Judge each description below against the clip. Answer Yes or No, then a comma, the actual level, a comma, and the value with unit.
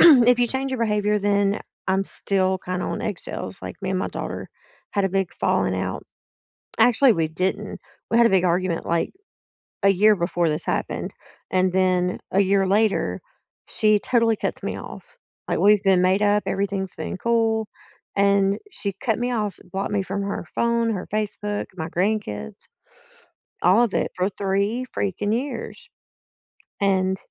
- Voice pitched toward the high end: Yes, high, 200 Hz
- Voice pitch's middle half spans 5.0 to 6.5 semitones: No, narrow, 2.6 semitones